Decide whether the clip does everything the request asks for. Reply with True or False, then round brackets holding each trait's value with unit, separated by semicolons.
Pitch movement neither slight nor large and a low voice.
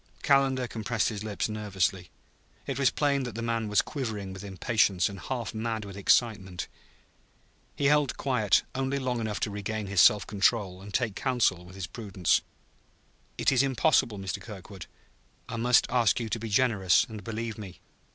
True (3.7 semitones; 110 Hz)